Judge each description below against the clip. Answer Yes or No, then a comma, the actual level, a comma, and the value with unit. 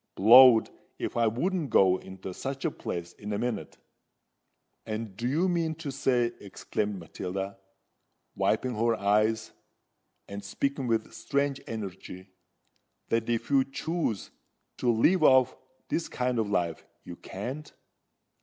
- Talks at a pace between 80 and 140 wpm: Yes, slow, 135 wpm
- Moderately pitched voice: No, low, 115 Hz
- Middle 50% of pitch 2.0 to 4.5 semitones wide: No, average, 5.0 semitones